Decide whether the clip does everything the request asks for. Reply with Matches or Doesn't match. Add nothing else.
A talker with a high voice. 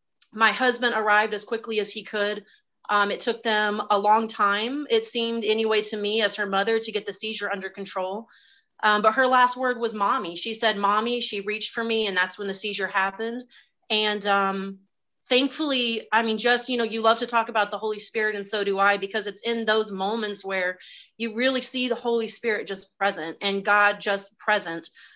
Matches